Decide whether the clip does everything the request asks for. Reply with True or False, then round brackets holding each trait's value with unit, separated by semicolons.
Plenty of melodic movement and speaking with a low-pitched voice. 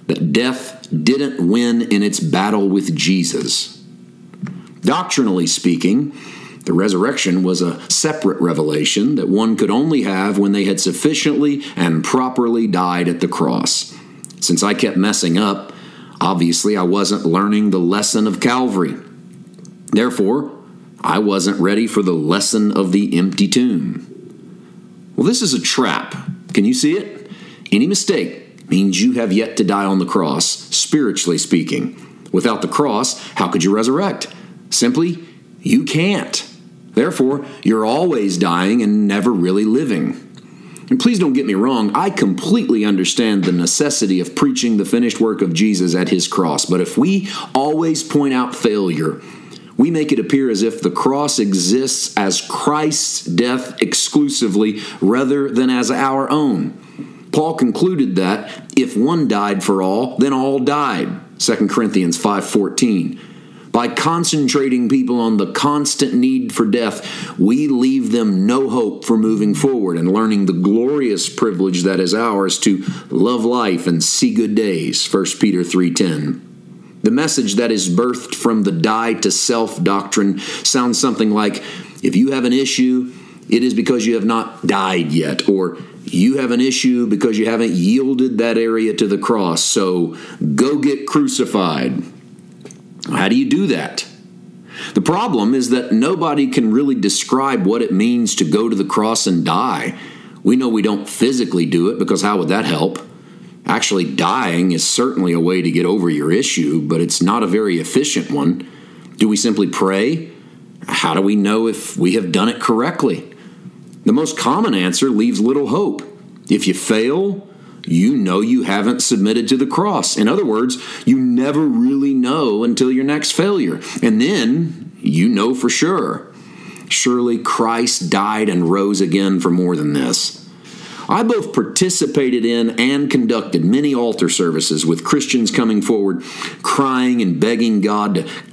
True (6.7 semitones; 115 Hz)